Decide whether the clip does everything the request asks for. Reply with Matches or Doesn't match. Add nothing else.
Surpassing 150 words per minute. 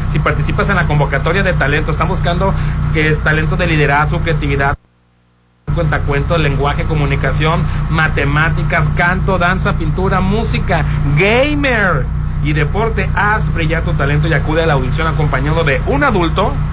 Doesn't match